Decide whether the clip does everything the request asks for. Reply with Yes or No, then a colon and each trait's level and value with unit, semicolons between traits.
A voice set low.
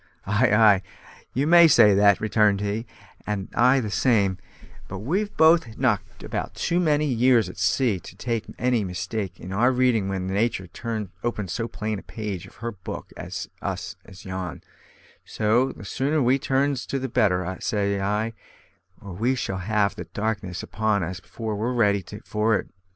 Yes: low, 110 Hz